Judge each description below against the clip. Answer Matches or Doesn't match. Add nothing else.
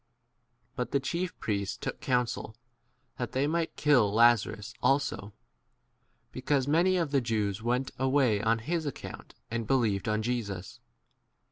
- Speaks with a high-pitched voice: Doesn't match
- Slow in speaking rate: Doesn't match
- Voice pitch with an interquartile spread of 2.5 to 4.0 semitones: Doesn't match